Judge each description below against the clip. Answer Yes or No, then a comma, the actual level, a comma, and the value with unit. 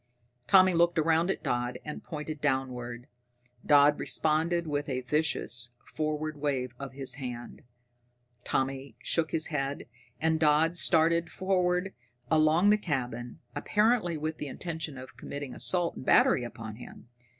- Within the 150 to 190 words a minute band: No, average, 140 wpm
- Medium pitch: Yes, medium, 150 Hz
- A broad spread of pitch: No, average, 3.9 semitones